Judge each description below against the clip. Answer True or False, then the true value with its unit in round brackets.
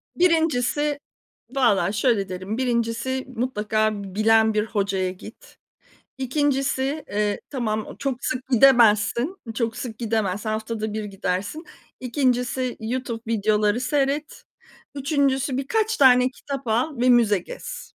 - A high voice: True (240 Hz)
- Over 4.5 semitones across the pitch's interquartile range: False (4.0 semitones)